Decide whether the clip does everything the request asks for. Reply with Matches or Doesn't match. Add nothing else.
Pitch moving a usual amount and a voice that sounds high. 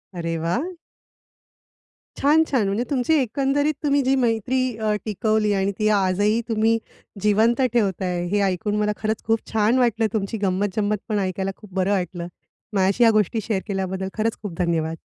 Matches